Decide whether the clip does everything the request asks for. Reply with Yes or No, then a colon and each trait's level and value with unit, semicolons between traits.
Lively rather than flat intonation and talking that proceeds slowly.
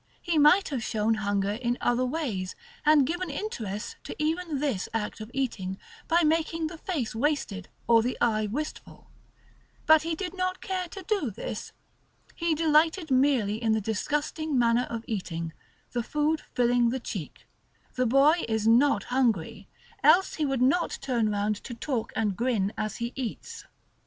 No: wide, 6.1 semitones; average, 165 wpm